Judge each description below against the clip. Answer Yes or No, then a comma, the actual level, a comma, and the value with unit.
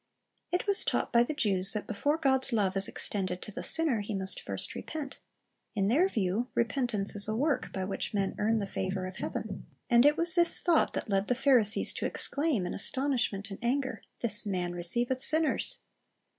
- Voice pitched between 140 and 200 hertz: No, high, 225 Hz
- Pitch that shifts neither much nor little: No, wide, 5.8 semitones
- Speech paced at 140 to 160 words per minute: No, average, 195 wpm